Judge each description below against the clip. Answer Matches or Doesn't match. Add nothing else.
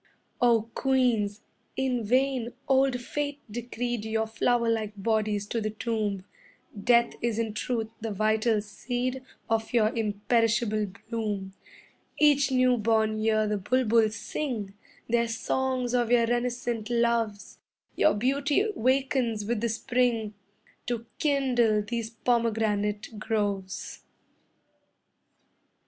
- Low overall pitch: Doesn't match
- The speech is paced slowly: Matches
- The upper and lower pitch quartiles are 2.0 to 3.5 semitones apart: Matches